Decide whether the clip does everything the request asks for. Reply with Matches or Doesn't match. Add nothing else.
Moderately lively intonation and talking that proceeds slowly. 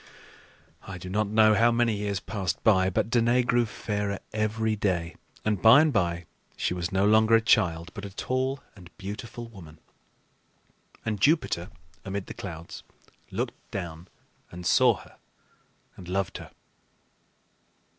Doesn't match